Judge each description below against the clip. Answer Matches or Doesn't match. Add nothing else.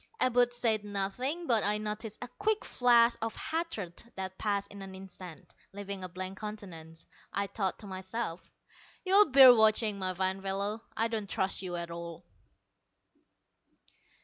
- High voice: Matches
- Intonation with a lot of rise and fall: Doesn't match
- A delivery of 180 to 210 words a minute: Doesn't match